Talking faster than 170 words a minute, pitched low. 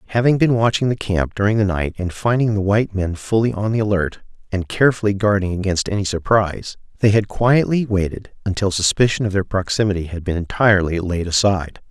Yes: average, 185 wpm; low, 100 Hz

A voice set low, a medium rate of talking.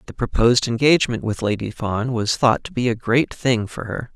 No: low, 120 Hz; fast, 215 wpm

